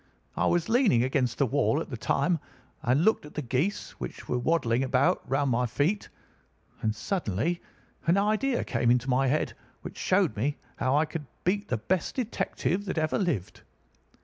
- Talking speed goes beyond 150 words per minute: Yes, average, 175 wpm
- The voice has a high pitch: No, medium, 145 Hz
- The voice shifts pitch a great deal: Yes, wide, 6.4 semitones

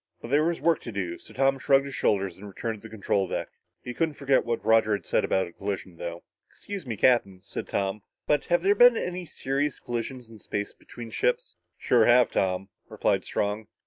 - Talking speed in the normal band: No, fast, 210 wpm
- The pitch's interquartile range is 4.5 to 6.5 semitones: Yes, wide, 5.6 semitones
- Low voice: Yes, low, 120 Hz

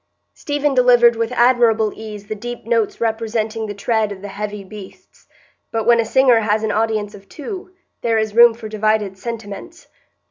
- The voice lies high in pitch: Yes, high, 220 Hz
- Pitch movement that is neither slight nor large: No, narrow, 2.1 semitones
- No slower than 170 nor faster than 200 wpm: Yes, average, 175 wpm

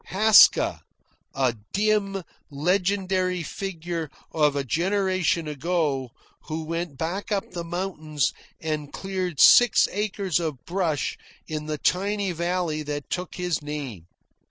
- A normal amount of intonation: Yes, average, 3.9 semitones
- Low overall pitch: No, medium, 170 Hz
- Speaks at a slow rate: Yes, slow, 120 wpm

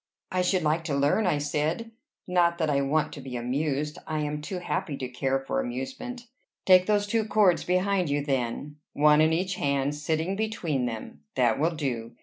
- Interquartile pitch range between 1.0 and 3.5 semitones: No, average, 4.7 semitones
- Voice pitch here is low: No, medium, 155 Hz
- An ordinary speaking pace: Yes, average, 190 wpm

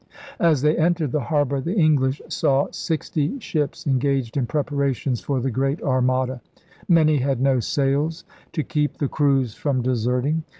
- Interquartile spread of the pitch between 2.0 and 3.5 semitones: Yes, average, 2.8 semitones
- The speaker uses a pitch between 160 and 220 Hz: No, medium, 140 Hz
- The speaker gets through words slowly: No, average, 160 wpm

